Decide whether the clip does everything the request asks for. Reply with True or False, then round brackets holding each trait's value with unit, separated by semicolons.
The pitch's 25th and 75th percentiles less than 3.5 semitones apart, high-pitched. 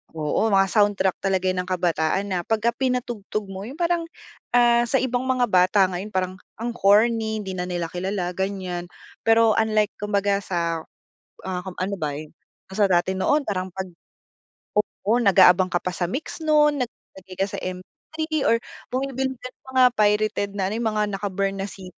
False (3.8 semitones; 200 Hz)